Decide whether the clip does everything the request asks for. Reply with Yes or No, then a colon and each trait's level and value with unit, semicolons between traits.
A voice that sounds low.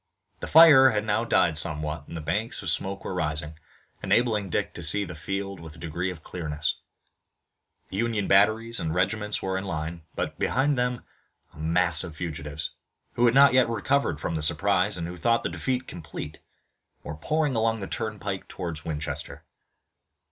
Yes: very low, 95 Hz